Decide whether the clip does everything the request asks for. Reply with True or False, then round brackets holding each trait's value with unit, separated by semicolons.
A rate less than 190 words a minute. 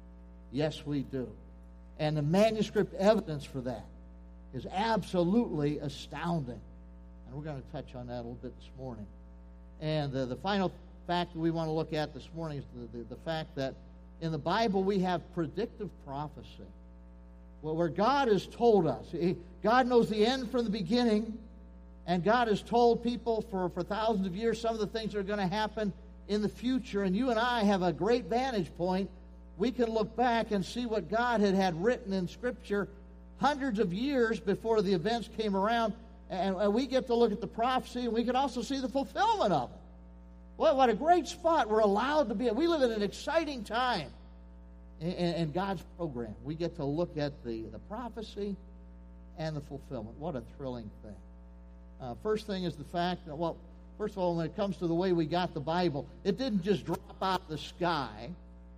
False (205 wpm)